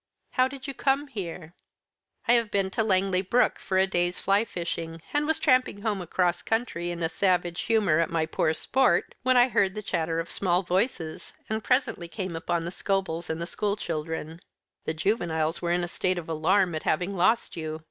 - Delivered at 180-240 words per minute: Yes, average, 200 wpm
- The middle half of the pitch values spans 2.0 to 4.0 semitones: No, average, 4.5 semitones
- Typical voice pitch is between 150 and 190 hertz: Yes, medium, 185 Hz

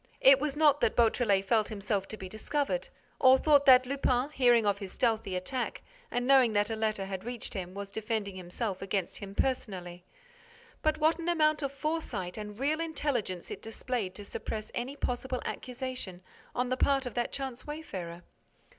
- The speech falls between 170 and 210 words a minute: Yes, average, 180 wpm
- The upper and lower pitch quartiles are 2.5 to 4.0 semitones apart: No, average, 5.3 semitones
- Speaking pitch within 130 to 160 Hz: No, high, 240 Hz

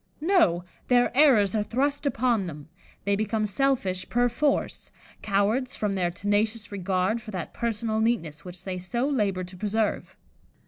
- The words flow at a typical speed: Yes, average, 150 wpm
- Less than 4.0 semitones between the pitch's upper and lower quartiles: No, average, 4.3 semitones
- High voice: Yes, high, 210 Hz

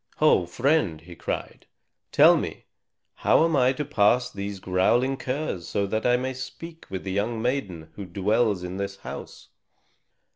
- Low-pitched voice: Yes, low, 105 Hz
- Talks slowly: No, average, 160 wpm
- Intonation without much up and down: No, wide, 5.5 semitones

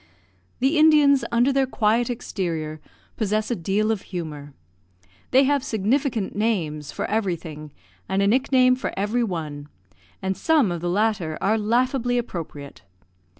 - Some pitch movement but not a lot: No, wide, 6.5 semitones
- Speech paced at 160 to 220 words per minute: No, average, 140 wpm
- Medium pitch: No, high, 215 Hz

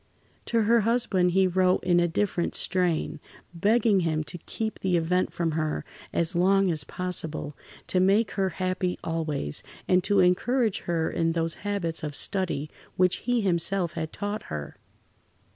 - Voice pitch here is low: No, medium, 180 Hz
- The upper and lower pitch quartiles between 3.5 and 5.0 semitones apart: No, average, 3.1 semitones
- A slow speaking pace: No, average, 160 wpm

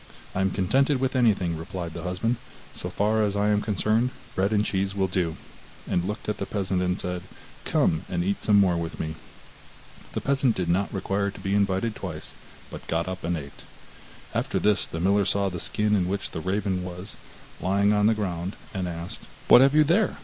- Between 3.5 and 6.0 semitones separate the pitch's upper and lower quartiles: No, average, 2.8 semitones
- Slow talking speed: No, fast, 205 wpm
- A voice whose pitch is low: Yes, very low, 95 Hz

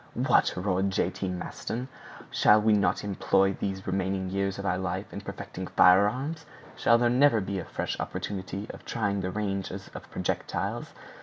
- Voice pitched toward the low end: Yes, low, 100 Hz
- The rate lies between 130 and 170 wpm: Yes, average, 165 wpm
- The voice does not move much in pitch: Yes, narrow, 1.9 semitones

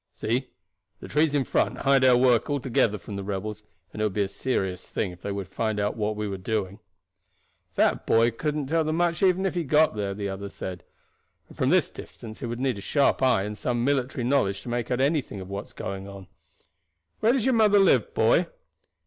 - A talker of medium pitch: No, low, 115 Hz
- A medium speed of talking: No, fast, 230 wpm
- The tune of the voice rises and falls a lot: Yes, wide, 6.0 semitones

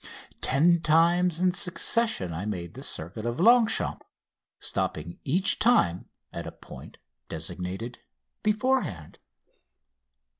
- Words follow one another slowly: Yes, slow, 105 wpm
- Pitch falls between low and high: Yes, medium, 160 Hz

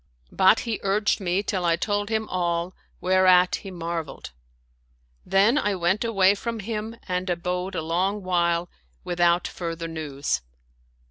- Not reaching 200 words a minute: Yes, average, 140 wpm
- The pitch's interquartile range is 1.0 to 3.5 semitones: Yes, average, 2.9 semitones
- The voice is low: No, medium, 185 Hz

